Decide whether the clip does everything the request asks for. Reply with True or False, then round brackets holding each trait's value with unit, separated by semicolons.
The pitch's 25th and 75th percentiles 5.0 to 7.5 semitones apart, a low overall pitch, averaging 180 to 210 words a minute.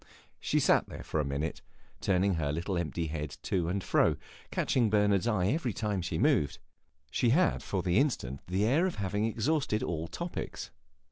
True (5.3 semitones; 95 Hz; 185 wpm)